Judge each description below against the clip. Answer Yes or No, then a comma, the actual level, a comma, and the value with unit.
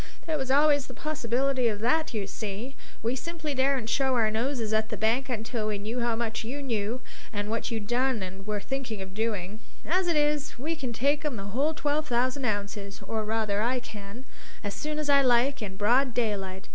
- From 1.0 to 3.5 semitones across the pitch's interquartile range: No, average, 4.4 semitones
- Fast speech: Yes, fast, 210 wpm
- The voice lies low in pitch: No, high, 235 Hz